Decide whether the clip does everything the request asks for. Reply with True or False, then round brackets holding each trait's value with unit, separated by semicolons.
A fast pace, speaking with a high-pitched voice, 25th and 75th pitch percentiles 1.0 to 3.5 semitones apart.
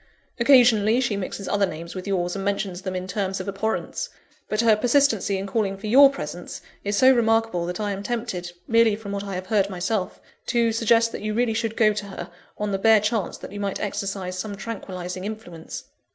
True (210 wpm; 205 Hz; 2.8 semitones)